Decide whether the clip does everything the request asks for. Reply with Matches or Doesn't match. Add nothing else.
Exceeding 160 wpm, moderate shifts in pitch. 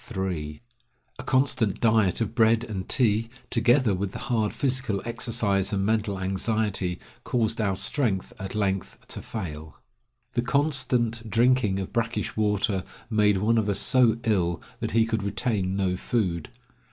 Doesn't match